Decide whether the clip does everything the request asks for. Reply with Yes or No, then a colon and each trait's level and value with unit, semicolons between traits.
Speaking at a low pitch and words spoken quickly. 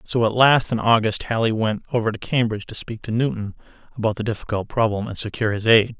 Yes: low, 110 Hz; fast, 220 wpm